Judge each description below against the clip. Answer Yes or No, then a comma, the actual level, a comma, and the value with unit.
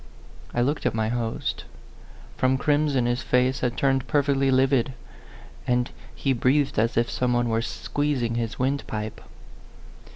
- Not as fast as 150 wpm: Yes, average, 140 wpm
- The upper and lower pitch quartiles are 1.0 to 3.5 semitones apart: Yes, narrow, 2.5 semitones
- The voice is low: Yes, low, 125 Hz